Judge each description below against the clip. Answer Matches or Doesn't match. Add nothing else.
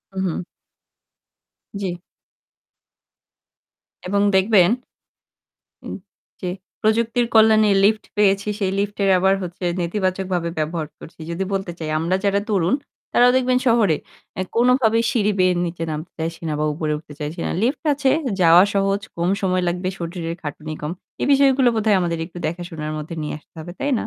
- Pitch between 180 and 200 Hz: Matches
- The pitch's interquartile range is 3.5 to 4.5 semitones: Matches